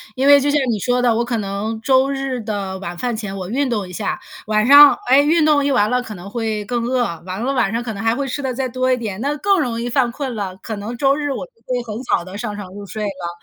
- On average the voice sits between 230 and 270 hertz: Yes, high, 235 Hz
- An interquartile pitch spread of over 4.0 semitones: Yes, average, 4.5 semitones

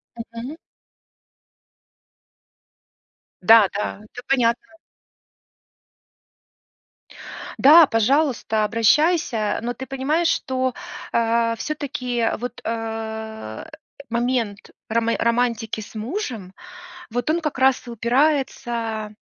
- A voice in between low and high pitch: No, high, 235 Hz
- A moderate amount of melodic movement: Yes, average, 3.0 semitones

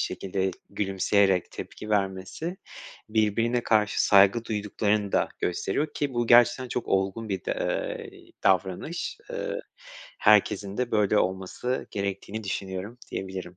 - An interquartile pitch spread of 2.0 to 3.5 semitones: Yes, average, 3.1 semitones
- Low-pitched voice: Yes, low, 105 Hz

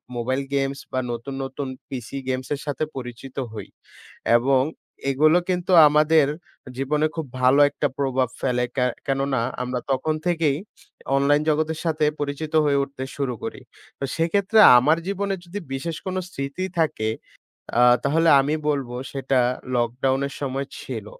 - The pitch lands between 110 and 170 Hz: Yes, medium, 140 Hz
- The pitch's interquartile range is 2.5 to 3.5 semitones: Yes, average, 2.9 semitones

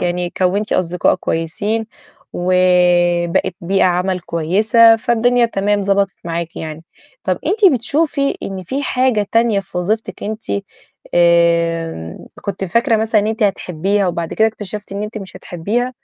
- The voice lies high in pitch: Yes, high, 195 Hz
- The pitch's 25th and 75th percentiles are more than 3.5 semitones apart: Yes, average, 4.0 semitones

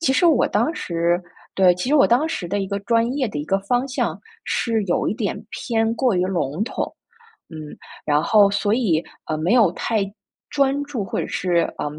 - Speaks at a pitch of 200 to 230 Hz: Yes, high, 210 Hz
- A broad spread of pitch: Yes, wide, 5.9 semitones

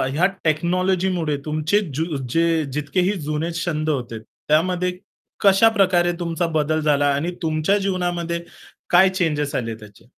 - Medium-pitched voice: Yes, medium, 165 Hz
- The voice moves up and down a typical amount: Yes, average, 3.1 semitones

